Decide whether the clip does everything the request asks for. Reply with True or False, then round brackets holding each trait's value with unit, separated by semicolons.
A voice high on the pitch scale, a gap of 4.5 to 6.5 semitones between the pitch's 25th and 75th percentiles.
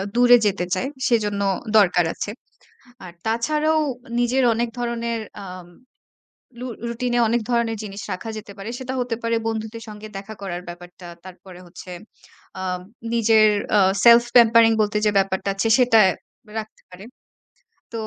False (220 Hz; 3.2 semitones)